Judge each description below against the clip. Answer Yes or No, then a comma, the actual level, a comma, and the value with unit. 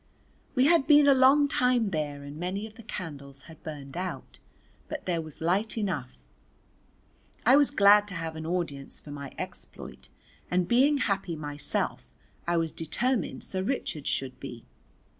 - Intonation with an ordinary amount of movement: No, wide, 8.1 semitones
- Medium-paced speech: Yes, average, 160 wpm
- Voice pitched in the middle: Yes, medium, 180 Hz